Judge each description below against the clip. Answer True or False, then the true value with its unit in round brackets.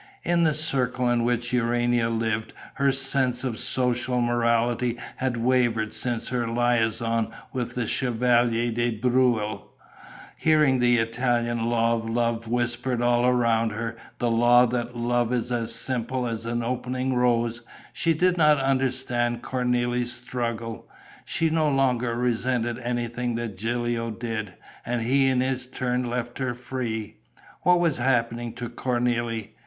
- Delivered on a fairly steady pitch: True (1.4 semitones)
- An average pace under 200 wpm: True (140 wpm)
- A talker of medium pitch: False (120 Hz)